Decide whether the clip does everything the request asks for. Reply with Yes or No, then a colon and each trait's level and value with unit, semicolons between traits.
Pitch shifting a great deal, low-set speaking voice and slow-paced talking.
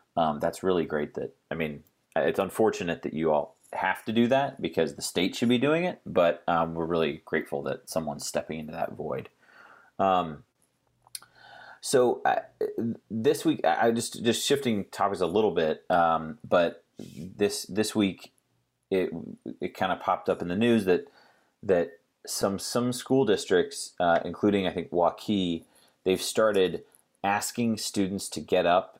No: wide, 7.9 semitones; low, 105 Hz; average, 165 wpm